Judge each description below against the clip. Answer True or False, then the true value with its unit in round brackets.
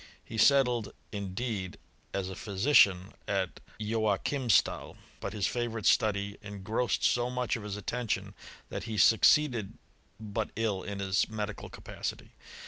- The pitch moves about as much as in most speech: True (3.1 semitones)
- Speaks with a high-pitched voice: False (105 Hz)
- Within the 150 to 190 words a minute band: False (135 wpm)